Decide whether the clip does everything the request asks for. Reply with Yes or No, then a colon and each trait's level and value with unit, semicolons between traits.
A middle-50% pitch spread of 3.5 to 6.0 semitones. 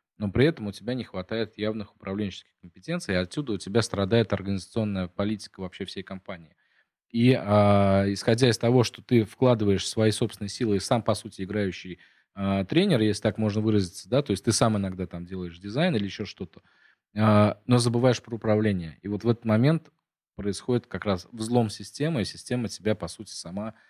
No: average, 3.1 semitones